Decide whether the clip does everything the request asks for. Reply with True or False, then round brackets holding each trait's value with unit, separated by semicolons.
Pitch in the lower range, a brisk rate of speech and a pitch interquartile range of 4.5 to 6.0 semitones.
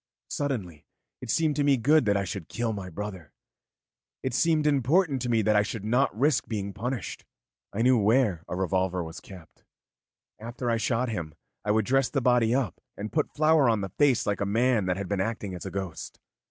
True (110 Hz; 210 wpm; 5.0 semitones)